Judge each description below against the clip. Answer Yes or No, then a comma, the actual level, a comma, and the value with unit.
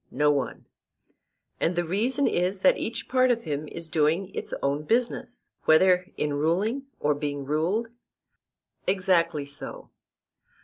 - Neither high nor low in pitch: Yes, medium, 175 Hz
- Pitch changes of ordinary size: No, wide, 5.7 semitones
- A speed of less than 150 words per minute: Yes, slow, 135 wpm